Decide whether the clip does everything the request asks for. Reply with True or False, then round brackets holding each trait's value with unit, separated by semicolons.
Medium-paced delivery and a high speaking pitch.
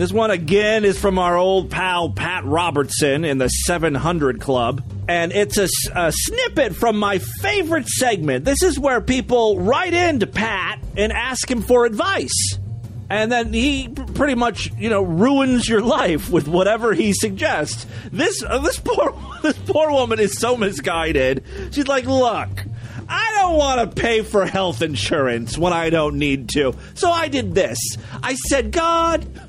True (170 wpm; 200 Hz)